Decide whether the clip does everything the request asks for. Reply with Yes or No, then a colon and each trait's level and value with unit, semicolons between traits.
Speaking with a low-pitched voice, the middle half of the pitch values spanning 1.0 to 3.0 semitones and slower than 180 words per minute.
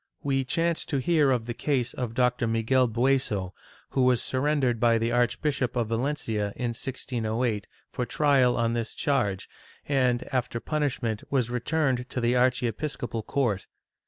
Yes: low, 125 Hz; average, 2.7 semitones; average, 150 wpm